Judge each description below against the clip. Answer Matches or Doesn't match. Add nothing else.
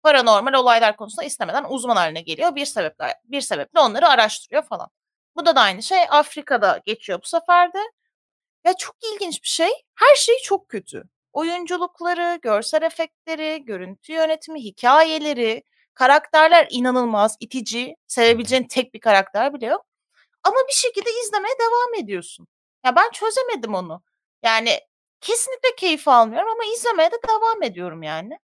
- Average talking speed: Doesn't match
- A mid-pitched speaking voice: Doesn't match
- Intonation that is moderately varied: Doesn't match